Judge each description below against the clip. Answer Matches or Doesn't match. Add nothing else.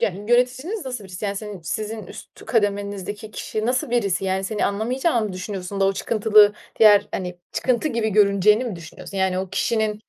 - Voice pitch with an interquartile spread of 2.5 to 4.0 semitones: Matches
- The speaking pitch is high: Matches